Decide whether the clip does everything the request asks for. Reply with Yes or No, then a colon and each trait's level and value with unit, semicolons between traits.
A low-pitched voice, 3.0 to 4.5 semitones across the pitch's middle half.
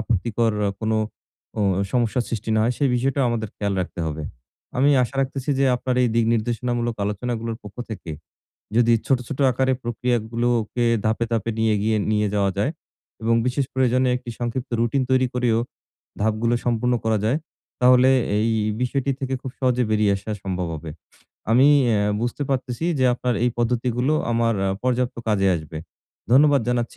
No: low, 120 Hz; narrow, 2.4 semitones